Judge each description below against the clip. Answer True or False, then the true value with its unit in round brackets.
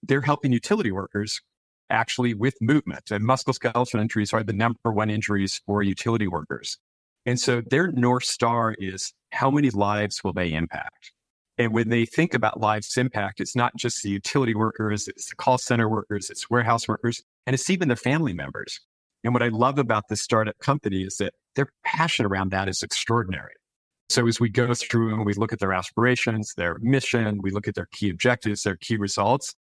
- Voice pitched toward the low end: True (115 Hz)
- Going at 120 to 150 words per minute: False (190 wpm)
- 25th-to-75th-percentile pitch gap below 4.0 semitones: True (3.2 semitones)